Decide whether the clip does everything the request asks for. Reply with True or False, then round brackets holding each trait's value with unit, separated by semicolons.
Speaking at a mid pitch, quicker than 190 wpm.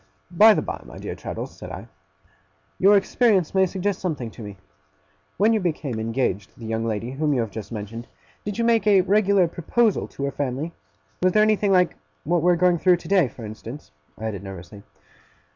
True (165 Hz; 200 wpm)